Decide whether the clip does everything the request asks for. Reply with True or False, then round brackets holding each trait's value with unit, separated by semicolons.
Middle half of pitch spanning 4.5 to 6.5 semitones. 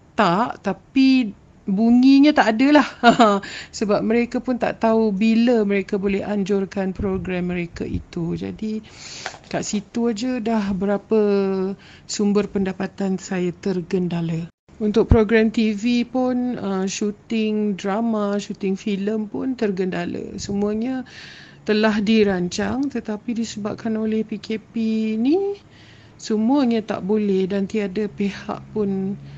False (2.7 semitones)